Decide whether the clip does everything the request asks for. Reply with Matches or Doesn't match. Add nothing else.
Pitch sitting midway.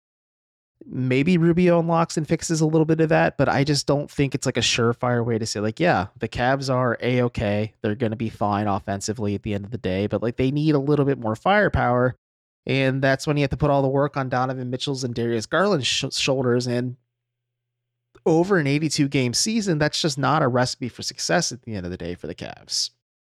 Doesn't match